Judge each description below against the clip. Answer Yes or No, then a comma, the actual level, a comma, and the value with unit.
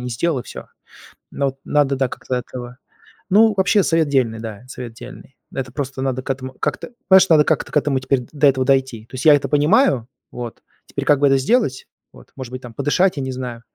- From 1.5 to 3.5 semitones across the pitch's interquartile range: Yes, average, 2.8 semitones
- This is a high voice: No, low, 135 Hz